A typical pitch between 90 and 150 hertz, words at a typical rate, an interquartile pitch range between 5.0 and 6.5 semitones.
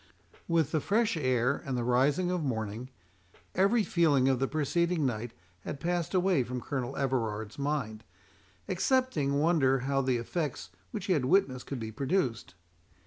Yes: medium, 140 Hz; average, 155 wpm; wide, 5.5 semitones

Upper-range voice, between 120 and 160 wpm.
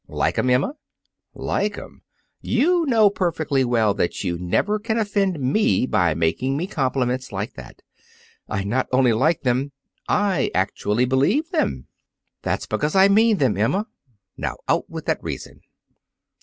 No: low, 135 Hz; average, 150 wpm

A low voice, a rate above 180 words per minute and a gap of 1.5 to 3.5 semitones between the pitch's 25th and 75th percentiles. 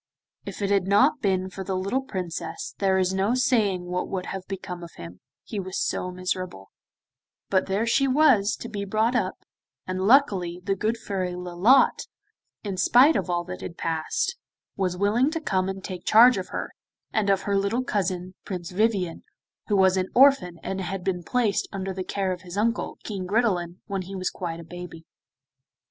No: high, 190 Hz; average, 190 wpm; average, 2.9 semitones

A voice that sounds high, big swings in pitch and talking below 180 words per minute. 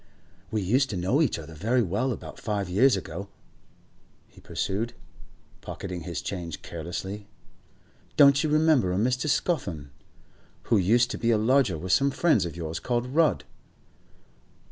No: low, 105 Hz; wide, 6.3 semitones; average, 150 wpm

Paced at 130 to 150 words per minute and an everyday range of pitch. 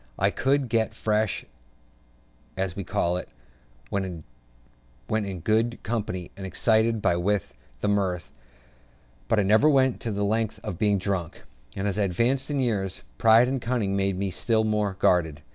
No: average, 160 wpm; average, 3.0 semitones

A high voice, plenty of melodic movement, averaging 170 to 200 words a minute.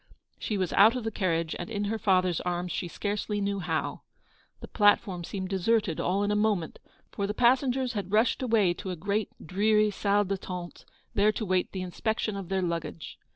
No: high, 200 Hz; average, 3.0 semitones; average, 195 wpm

